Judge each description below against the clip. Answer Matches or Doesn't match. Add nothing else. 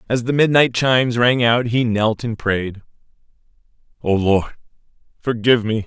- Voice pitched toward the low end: Matches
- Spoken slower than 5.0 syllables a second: Matches